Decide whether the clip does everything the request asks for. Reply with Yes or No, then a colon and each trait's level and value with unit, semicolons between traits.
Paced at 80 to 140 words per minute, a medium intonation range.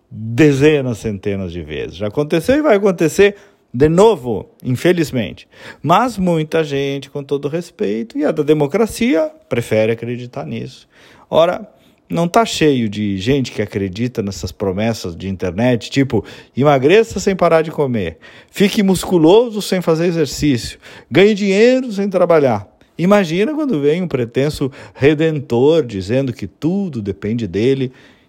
No: average, 135 wpm; wide, 7.7 semitones